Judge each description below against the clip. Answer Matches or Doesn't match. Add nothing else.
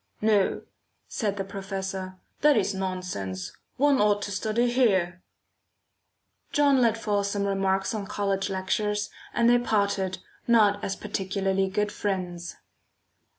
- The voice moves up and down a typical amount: Doesn't match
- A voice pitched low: Doesn't match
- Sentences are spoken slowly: Matches